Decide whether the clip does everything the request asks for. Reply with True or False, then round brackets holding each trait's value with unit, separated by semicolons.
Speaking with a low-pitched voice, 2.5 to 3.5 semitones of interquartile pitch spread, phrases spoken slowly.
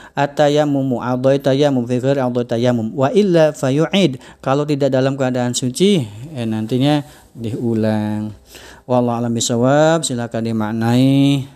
False (130 Hz; 3.2 semitones; 120 wpm)